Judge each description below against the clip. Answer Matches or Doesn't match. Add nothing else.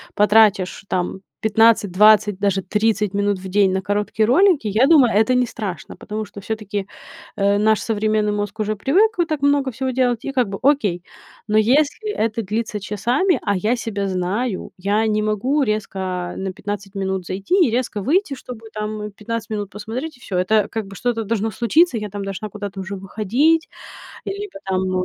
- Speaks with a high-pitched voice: Matches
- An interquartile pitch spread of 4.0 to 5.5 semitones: Doesn't match